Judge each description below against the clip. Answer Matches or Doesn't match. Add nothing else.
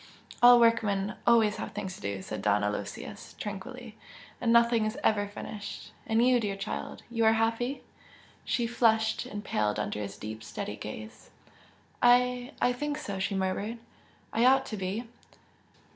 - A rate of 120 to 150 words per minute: Doesn't match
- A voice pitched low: Doesn't match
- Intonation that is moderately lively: Matches